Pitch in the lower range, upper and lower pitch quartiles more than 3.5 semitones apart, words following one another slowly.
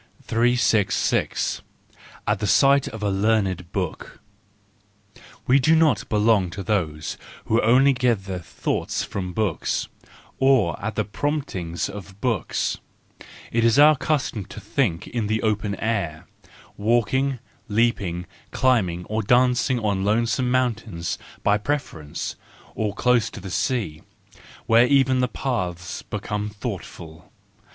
Yes: low, 110 Hz; average, 4.5 semitones; slow, 120 wpm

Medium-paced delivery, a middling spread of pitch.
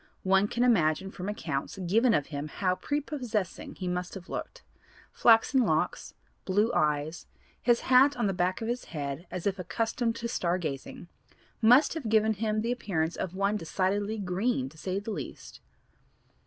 Yes: average, 170 wpm; average, 4.4 semitones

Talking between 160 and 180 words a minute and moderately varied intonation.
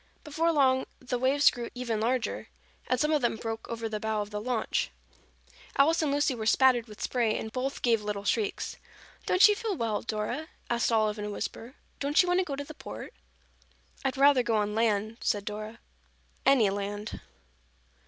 No: average, 190 wpm; average, 4.4 semitones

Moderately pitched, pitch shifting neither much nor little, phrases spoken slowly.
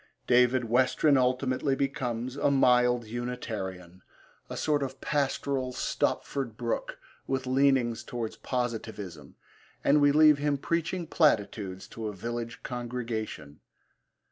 No: low, 125 Hz; average, 3.3 semitones; slow, 115 wpm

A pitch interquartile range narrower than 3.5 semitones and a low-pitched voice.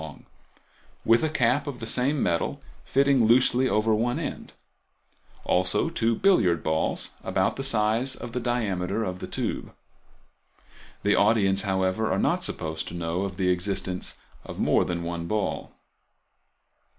No: average, 5.1 semitones; low, 105 Hz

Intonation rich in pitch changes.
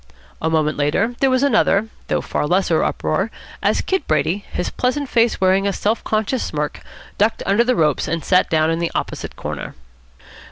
Yes: wide, 6.3 semitones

